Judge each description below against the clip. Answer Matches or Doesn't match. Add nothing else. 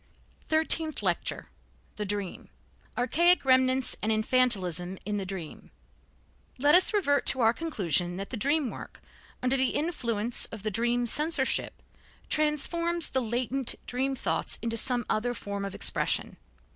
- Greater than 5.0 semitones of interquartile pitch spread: Matches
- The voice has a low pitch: Doesn't match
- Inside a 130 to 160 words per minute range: Matches